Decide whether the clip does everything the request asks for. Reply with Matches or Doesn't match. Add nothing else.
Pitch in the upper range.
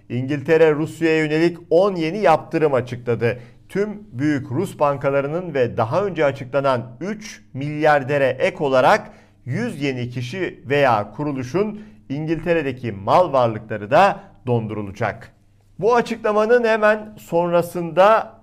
Doesn't match